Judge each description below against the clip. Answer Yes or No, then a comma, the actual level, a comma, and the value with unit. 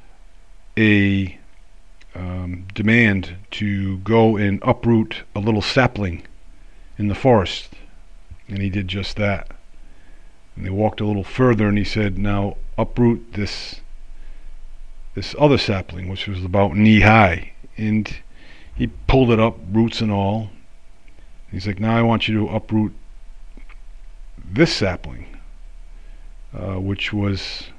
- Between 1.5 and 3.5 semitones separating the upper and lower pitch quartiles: Yes, average, 2.9 semitones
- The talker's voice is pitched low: Yes, low, 100 Hz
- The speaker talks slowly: Yes, slow, 125 wpm